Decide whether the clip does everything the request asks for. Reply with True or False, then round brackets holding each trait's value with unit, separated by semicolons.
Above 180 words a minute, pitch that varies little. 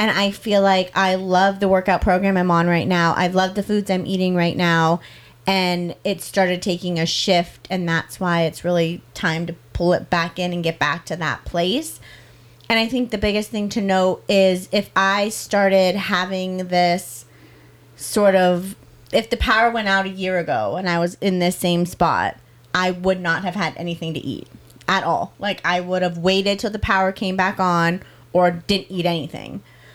True (200 wpm; 2.2 semitones)